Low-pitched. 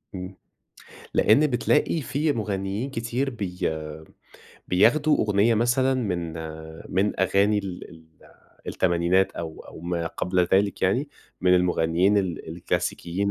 Yes: low, 100 Hz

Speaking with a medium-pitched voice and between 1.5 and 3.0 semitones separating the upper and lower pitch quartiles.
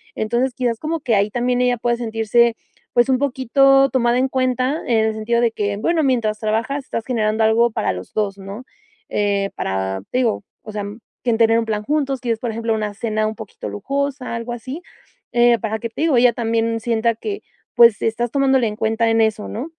No: high, 230 Hz; narrow, 2.6 semitones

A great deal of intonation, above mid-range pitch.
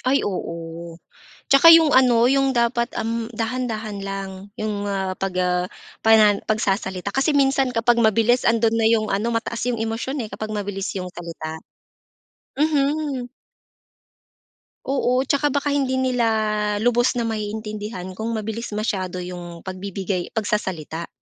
No: average, 4.2 semitones; high, 220 Hz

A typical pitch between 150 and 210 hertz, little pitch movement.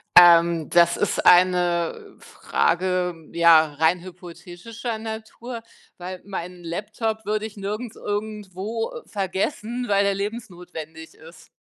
No: medium, 185 Hz; average, 3.8 semitones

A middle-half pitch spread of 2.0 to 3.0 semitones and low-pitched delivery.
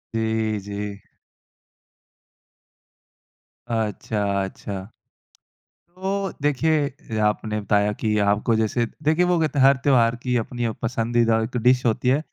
No: average, 4.0 semitones; low, 115 Hz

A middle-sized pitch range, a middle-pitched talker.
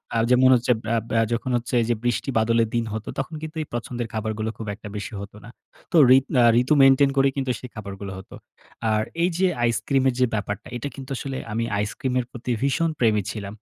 No: average, 3.3 semitones; low, 120 Hz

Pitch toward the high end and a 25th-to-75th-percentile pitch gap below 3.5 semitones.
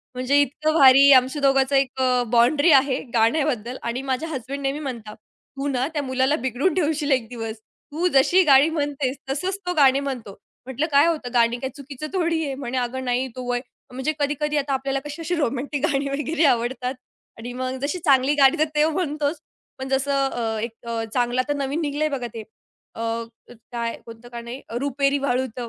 Yes: very high, 270 Hz; average, 2.8 semitones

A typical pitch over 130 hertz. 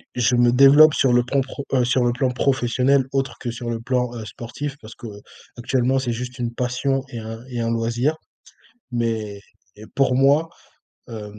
No: low, 125 Hz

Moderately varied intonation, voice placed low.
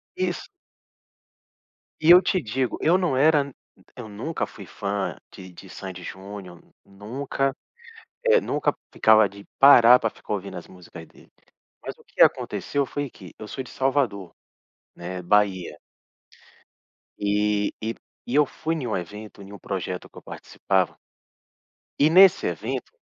No: wide, 6.4 semitones; low, 110 Hz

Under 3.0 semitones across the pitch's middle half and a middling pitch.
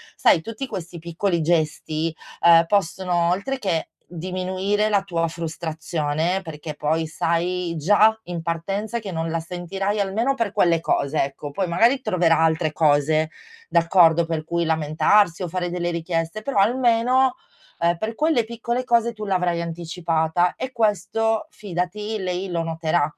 No: average, 4.0 semitones; medium, 175 Hz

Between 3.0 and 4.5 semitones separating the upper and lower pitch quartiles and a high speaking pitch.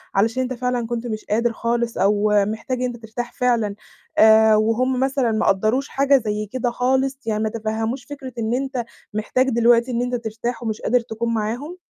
No: narrow, 2.4 semitones; high, 235 Hz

